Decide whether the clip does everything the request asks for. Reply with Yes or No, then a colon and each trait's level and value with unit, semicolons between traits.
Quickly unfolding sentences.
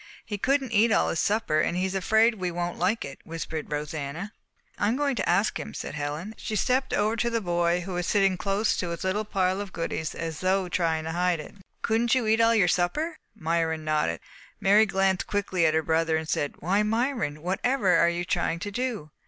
Yes: fast, 220 wpm